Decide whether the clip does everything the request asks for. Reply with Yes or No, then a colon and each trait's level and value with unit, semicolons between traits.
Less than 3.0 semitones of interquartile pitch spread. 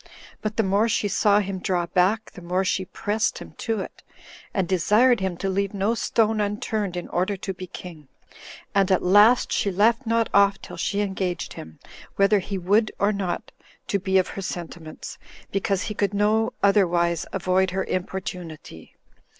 Yes: narrow, 2.4 semitones